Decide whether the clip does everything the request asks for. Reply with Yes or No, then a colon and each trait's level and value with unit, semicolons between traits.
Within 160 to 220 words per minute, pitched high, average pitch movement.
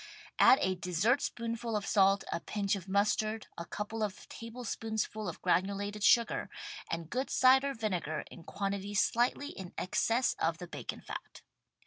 No: average, 150 wpm; high, 205 Hz; average, 3.4 semitones